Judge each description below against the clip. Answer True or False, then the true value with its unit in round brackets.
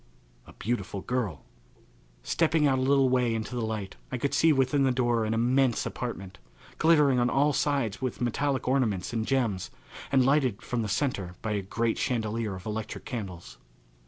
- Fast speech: False (175 wpm)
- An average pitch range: True (3.8 semitones)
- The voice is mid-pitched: False (120 Hz)